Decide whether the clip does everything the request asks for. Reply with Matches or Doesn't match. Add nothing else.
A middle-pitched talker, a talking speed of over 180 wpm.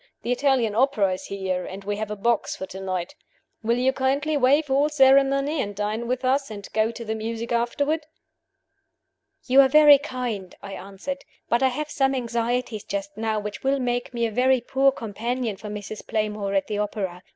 Doesn't match